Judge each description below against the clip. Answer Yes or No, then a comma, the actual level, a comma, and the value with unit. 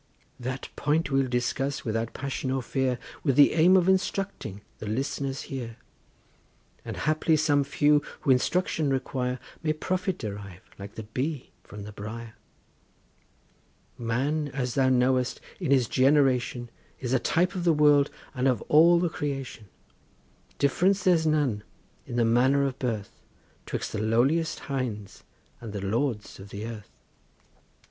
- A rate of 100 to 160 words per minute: Yes, average, 145 wpm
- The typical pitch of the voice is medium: No, low, 130 Hz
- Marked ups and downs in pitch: No, average, 4.2 semitones